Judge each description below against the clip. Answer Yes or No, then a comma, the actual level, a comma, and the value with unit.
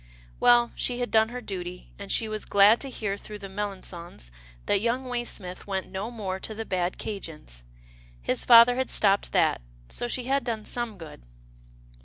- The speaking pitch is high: Yes, high, 210 Hz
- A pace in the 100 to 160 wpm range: No, average, 180 wpm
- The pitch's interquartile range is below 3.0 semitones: No, average, 4.0 semitones